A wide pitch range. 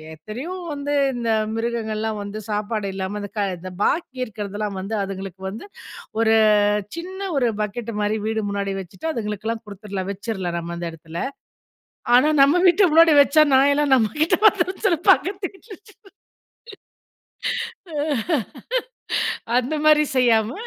Yes: wide, 6.3 semitones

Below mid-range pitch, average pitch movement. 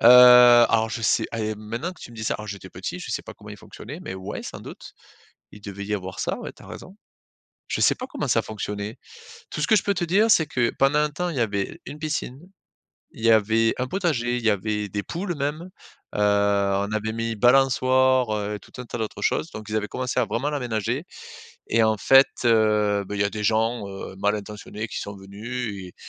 Yes: low, 110 Hz; average, 3.6 semitones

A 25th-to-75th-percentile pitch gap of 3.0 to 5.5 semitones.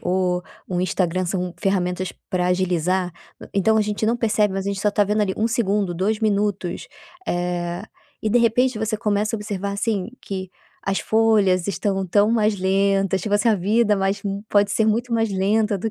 No: narrow, 2.4 semitones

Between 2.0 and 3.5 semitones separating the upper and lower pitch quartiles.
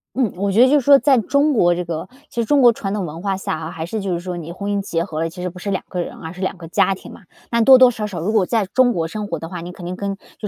No: average, 4.4 semitones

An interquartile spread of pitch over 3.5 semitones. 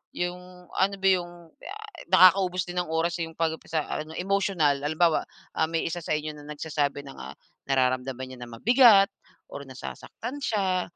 Yes: average, 4.2 semitones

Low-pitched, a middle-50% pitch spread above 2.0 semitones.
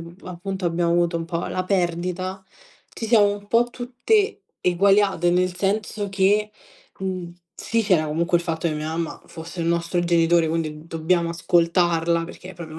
No: medium, 175 Hz; narrow, 2.4 semitones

